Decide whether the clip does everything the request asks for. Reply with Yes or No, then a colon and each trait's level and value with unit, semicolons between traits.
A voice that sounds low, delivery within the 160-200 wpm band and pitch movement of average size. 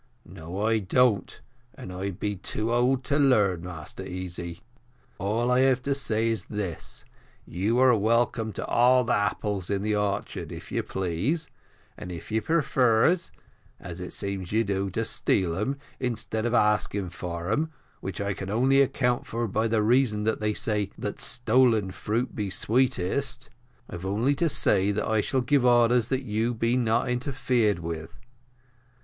Yes: low, 110 Hz; average, 165 wpm; average, 4.0 semitones